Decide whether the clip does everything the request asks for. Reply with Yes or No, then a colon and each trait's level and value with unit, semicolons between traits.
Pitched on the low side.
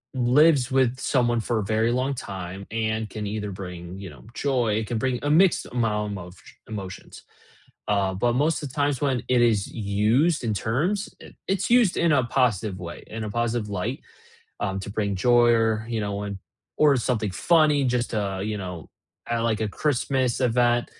Yes: low, 115 Hz